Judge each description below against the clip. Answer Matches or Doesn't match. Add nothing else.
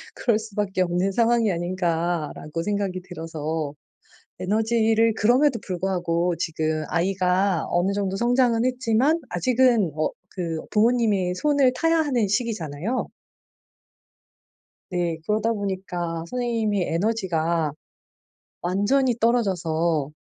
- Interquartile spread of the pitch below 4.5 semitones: Doesn't match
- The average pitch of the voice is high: Matches